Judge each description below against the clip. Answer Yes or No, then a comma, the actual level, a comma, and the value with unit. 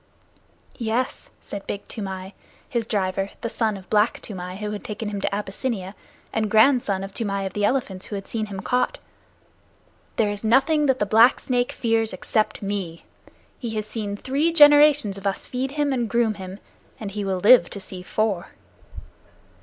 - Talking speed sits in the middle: Yes, average, 175 wpm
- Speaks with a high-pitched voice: Yes, high, 215 Hz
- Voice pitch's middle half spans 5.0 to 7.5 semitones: No, average, 3.4 semitones